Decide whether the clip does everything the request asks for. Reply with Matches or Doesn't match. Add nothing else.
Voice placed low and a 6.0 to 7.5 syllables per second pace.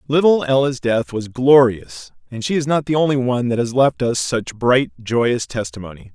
Doesn't match